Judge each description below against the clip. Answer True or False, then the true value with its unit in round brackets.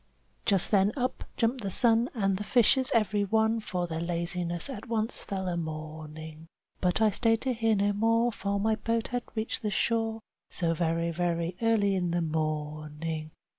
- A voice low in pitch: False (200 Hz)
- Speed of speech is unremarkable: True (175 wpm)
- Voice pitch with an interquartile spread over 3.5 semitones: True (5.1 semitones)